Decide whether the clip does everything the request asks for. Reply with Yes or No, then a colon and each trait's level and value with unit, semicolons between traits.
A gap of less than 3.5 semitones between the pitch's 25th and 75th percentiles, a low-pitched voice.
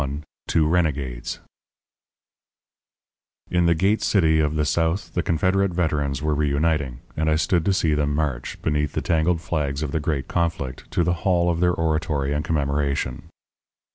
Yes: average, 2.8 semitones; very low, 80 Hz